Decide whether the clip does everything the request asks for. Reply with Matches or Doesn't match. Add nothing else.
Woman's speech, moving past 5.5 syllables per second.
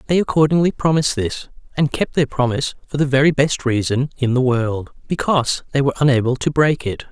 Doesn't match